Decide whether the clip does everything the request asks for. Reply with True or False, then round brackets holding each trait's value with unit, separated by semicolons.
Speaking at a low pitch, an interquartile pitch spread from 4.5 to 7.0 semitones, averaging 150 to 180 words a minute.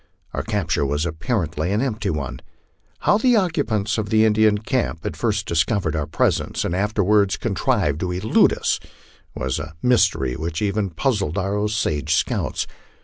True (100 Hz; 5.1 semitones; 155 wpm)